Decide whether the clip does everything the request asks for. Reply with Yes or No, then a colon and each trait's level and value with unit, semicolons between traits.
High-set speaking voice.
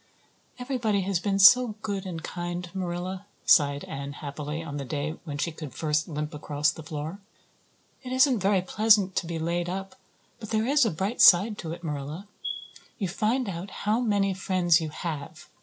No: medium, 180 Hz